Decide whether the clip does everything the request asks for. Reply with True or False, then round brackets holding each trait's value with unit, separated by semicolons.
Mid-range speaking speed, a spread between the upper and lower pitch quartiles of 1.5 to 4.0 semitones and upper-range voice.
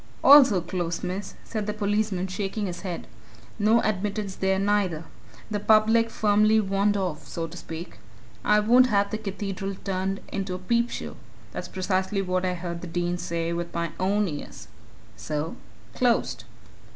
True (155 wpm; 2.9 semitones; 195 Hz)